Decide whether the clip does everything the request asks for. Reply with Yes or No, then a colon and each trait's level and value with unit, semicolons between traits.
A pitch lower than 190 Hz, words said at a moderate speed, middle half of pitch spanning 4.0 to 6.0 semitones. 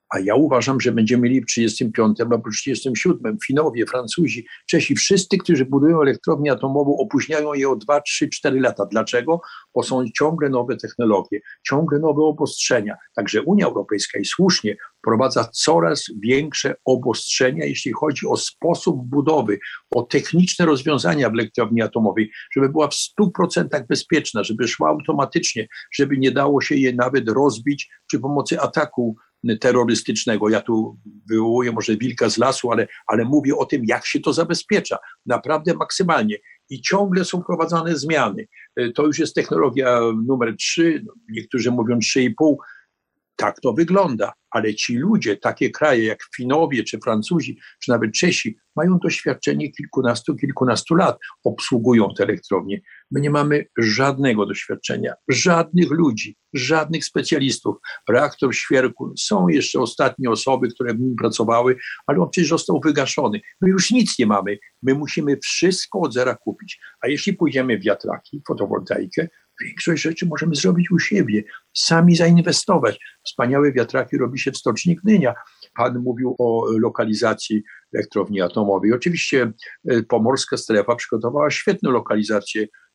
Yes: medium, 140 Hz; average, 140 wpm; wide, 5.5 semitones